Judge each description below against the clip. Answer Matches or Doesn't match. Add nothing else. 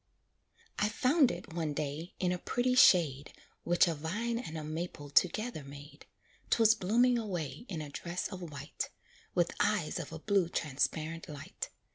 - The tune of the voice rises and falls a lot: Matches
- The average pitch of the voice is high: Doesn't match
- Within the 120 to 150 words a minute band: Doesn't match